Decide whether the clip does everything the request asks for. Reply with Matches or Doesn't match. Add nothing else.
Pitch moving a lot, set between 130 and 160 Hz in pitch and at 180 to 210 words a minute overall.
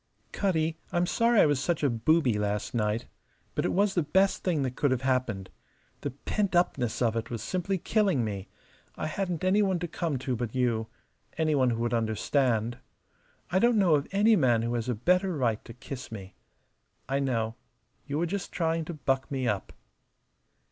Matches